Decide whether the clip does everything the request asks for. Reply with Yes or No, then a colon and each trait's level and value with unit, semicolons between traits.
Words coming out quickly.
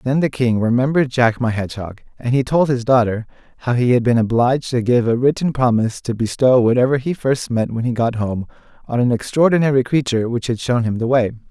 Yes: fast, 220 wpm